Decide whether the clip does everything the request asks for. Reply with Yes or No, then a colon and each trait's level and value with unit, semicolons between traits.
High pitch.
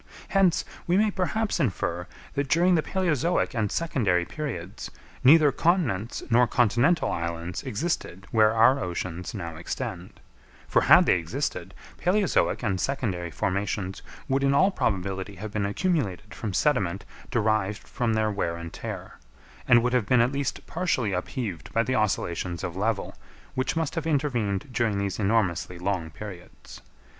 No: low, 110 Hz